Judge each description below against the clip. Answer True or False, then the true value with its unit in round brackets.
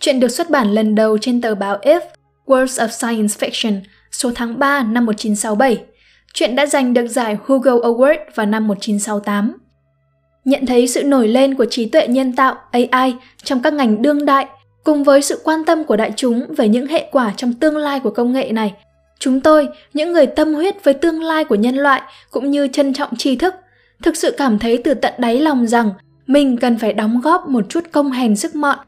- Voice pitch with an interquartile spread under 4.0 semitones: False (4.3 semitones)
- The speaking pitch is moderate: False (260 Hz)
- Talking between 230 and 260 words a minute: False (210 wpm)